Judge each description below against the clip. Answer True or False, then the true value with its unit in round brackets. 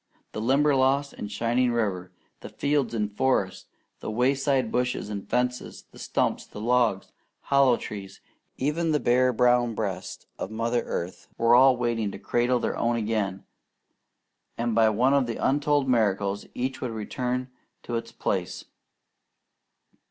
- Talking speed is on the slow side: False (145 wpm)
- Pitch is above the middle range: False (120 Hz)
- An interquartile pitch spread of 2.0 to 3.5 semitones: True (3.0 semitones)